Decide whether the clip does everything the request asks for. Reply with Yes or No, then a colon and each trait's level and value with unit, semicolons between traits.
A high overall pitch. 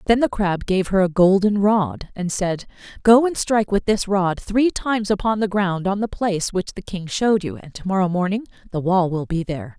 Yes: high, 195 Hz